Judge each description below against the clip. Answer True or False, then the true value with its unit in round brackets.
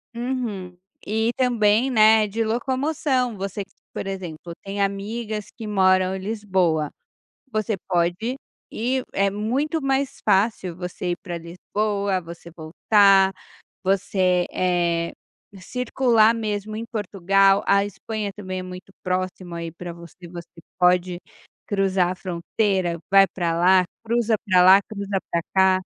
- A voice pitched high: True (195 Hz)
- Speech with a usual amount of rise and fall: True (3.2 semitones)